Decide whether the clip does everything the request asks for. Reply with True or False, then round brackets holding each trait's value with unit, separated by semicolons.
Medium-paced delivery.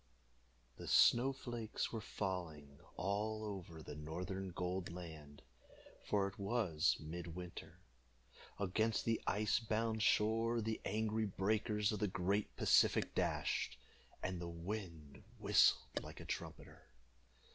False (125 wpm)